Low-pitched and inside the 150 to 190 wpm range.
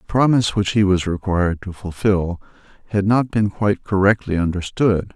Yes: low, 100 Hz; average, 165 wpm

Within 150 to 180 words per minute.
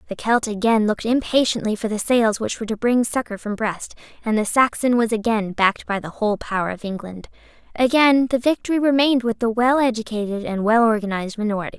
No: average, 200 wpm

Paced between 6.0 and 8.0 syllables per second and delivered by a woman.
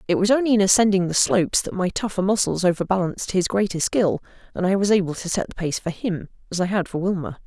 Yes: 6.4 syllables/s; female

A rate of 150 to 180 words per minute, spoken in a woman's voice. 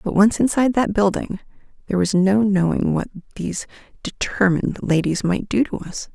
Yes: average, 165 wpm; female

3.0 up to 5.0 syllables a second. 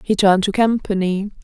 No: 5.7 syllables/s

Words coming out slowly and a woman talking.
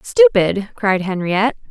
Yes: slow, 105 wpm; female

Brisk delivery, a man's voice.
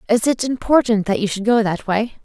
No: fast, 240 wpm; female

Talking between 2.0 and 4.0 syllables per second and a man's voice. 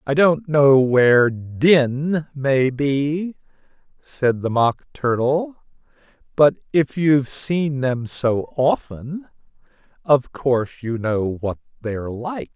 Yes: 3.2 syllables/s; male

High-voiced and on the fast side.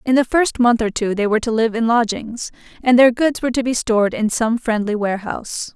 Yes: high, 230 Hz; fast, 240 wpm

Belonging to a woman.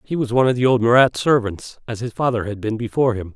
No: male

